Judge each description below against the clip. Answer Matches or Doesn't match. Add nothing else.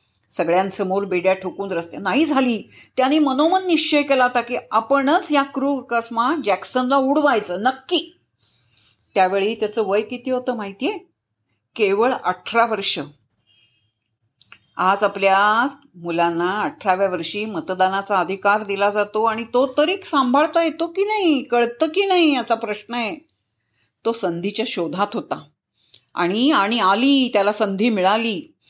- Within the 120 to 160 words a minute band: Matches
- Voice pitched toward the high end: Matches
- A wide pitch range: Matches